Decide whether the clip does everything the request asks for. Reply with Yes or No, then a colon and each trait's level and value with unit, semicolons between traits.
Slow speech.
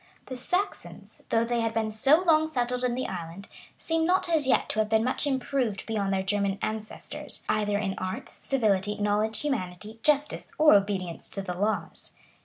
No: average, 185 wpm